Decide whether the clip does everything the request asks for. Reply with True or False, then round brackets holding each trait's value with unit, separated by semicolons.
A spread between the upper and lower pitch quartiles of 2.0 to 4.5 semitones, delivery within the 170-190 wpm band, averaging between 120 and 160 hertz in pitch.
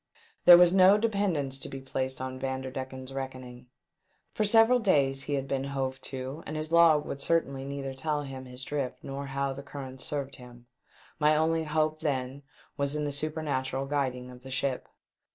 True (2.7 semitones; 185 wpm; 140 Hz)